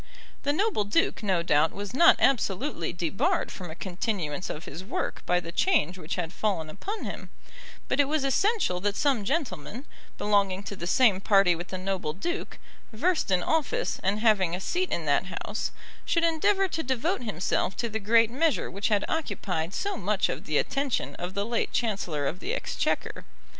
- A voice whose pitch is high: Yes, high, 205 Hz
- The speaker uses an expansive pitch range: Yes, wide, 7.7 semitones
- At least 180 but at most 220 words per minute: Yes, average, 185 wpm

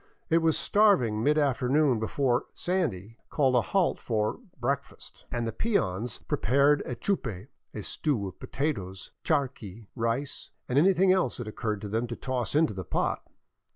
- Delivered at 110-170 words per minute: No, average, 180 wpm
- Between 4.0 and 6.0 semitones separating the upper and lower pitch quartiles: Yes, average, 5.3 semitones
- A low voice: Yes, low, 125 Hz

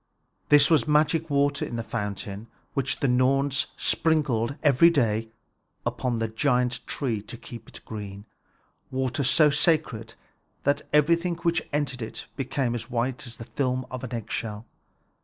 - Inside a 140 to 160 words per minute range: Yes, average, 145 wpm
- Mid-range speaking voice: No, low, 130 Hz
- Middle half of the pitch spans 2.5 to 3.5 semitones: No, average, 4.0 semitones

